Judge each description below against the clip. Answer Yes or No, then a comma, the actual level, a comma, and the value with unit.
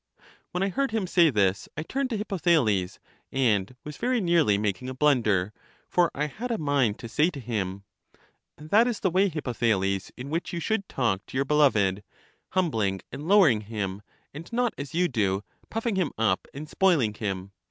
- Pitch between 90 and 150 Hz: Yes, medium, 140 Hz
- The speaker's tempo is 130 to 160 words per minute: No, average, 185 wpm